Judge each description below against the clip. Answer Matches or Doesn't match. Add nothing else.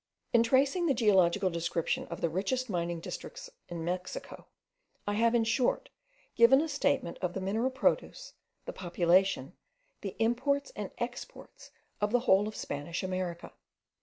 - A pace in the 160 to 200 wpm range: Doesn't match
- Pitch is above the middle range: Matches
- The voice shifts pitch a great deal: Matches